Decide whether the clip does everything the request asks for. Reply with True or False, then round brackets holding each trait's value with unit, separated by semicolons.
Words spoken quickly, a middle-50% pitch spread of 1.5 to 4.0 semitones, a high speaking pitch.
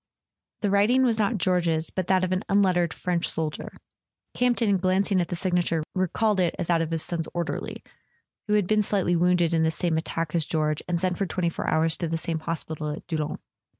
False (215 wpm; 2.8 semitones; 175 Hz)